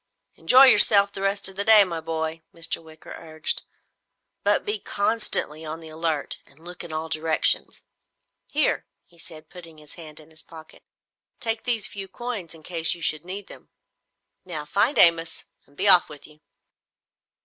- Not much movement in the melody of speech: No, average, 4.0 semitones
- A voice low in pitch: No, medium, 165 Hz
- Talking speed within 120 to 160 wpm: No, average, 170 wpm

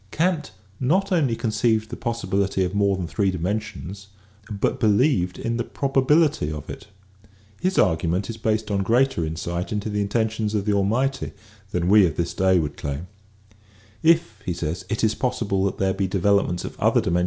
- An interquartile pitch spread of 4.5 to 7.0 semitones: No, average, 4.0 semitones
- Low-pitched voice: Yes, low, 100 Hz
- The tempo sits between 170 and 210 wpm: Yes, average, 175 wpm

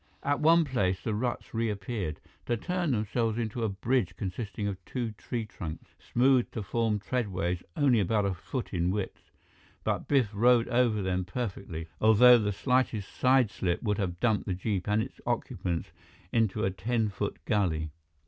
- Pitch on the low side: Yes, low, 110 Hz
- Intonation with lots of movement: No, average, 4.1 semitones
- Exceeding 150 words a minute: Yes, average, 165 wpm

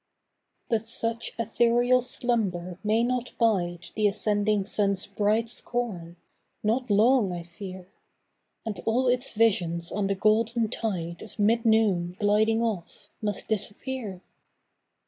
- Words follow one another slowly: Yes, slow, 125 wpm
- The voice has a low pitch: No, high, 215 Hz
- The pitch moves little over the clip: No, average, 3.1 semitones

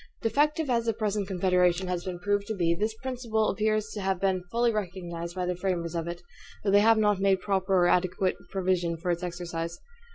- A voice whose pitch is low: No, high, 190 Hz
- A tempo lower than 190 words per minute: No, fast, 205 wpm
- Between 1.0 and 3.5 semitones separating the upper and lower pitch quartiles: Yes, average, 3.2 semitones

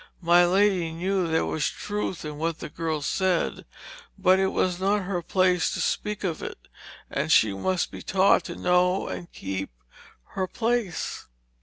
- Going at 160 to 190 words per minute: Yes, average, 165 wpm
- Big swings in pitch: No, narrow, 2.6 semitones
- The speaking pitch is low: No, medium, 180 Hz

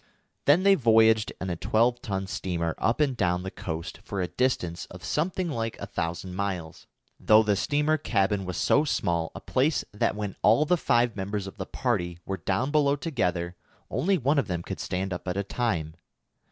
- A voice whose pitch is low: Yes, low, 105 Hz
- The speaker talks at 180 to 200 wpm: Yes, average, 195 wpm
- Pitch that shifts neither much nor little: No, wide, 6.3 semitones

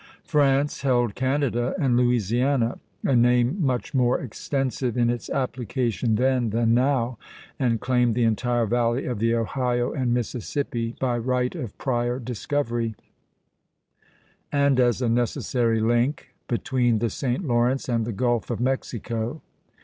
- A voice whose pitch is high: No, low, 120 Hz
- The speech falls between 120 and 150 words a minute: Yes, slow, 135 wpm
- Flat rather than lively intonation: Yes, narrow, 1.9 semitones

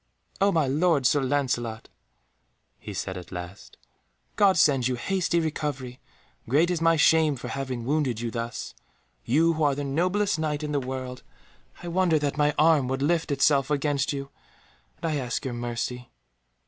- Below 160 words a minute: No, average, 170 wpm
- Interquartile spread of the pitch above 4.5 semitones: No, average, 4.0 semitones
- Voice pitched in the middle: Yes, medium, 145 Hz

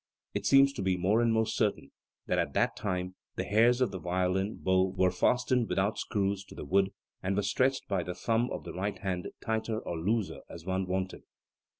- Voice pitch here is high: No, low, 100 Hz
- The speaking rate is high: Yes, fast, 210 wpm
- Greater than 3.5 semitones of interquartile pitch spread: No, average, 3.2 semitones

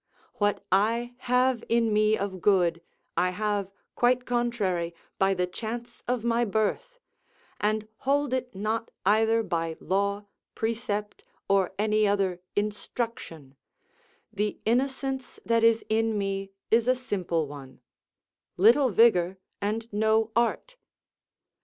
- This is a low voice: No, high, 215 Hz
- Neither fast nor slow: No, slow, 120 wpm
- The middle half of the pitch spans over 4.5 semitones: No, average, 3.3 semitones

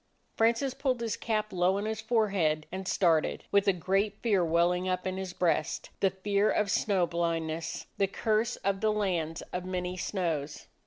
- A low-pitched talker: No, high, 190 Hz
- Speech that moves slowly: No, average, 175 wpm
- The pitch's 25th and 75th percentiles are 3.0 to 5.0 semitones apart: Yes, average, 3.5 semitones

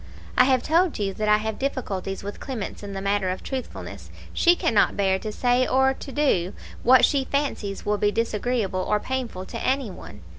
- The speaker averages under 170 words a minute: No, average, 195 wpm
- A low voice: No, high, 220 Hz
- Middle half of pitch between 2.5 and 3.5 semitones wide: No, average, 4.8 semitones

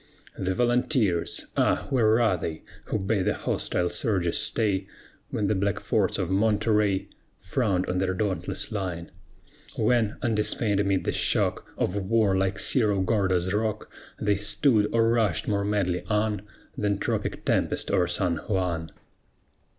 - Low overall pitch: Yes, low, 100 Hz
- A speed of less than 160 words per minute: Yes, average, 145 wpm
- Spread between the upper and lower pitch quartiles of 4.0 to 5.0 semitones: No, average, 2.7 semitones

